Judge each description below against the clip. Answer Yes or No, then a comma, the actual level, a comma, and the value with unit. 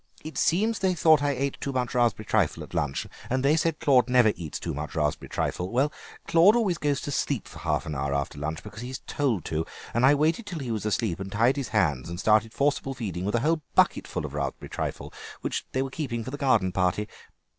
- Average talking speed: No, fast, 230 wpm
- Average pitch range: No, wide, 7.5 semitones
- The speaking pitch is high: No, low, 120 Hz